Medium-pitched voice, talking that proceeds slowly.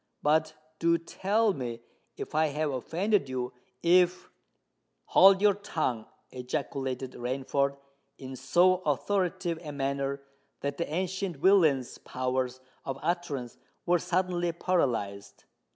Yes: medium, 155 Hz; slow, 105 wpm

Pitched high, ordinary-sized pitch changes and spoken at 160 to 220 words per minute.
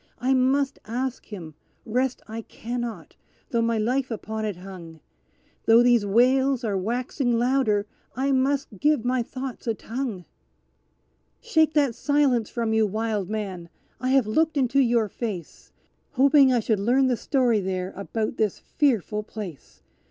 No: high, 235 Hz; average, 3.7 semitones; average, 150 wpm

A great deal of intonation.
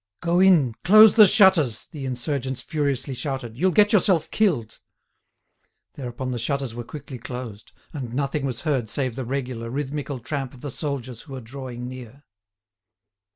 No: average, 3.5 semitones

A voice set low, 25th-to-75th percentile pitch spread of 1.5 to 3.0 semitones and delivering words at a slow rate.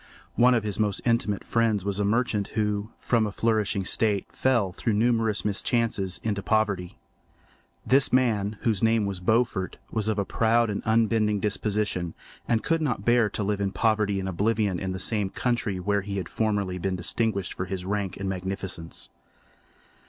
No: low, 105 Hz; narrow, 2.5 semitones; average, 175 wpm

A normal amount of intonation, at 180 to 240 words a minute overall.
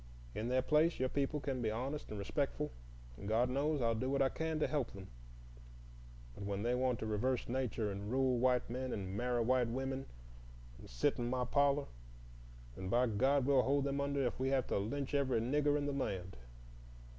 Yes: average, 3.3 semitones; fast, 205 wpm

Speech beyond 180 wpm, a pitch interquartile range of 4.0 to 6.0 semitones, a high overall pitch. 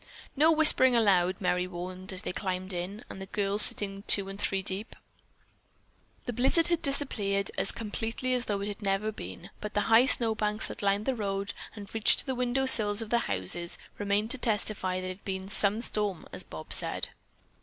No: average, 195 wpm; average, 2.9 semitones; high, 205 Hz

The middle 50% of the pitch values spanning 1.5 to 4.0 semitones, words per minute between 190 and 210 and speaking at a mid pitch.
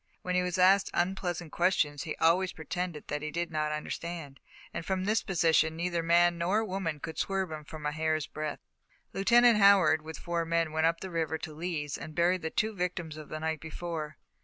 Yes: narrow, 2.6 semitones; average, 200 wpm; medium, 170 Hz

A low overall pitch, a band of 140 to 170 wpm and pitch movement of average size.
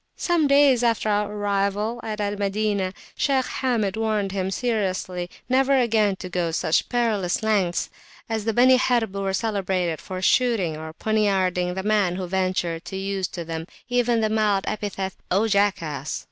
No: high, 205 Hz; average, 160 wpm; average, 3.3 semitones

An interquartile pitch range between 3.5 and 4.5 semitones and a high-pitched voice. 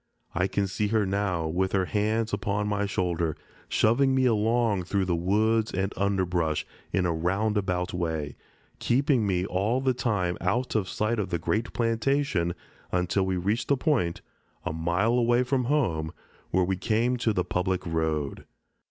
No: average, 4.2 semitones; low, 100 Hz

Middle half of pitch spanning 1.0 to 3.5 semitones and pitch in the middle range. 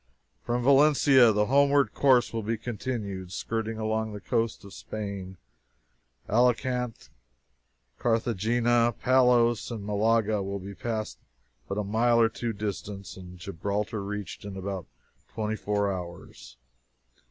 No: average, 3.0 semitones; low, 110 Hz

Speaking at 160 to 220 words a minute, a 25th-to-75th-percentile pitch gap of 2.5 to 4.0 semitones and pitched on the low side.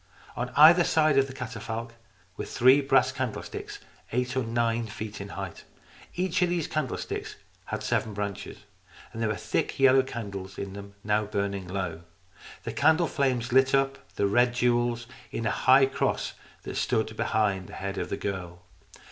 No: average, 165 wpm; average, 4.7 semitones; low, 115 Hz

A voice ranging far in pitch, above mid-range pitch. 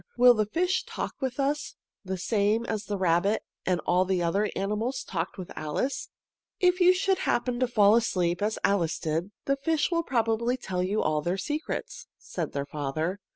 Yes: wide, 6.2 semitones; high, 210 Hz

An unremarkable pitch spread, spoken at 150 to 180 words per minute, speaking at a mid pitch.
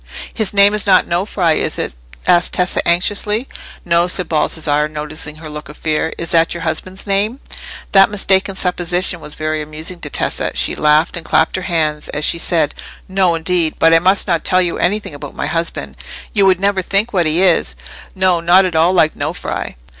No: average, 3.2 semitones; average, 190 wpm; medium, 175 Hz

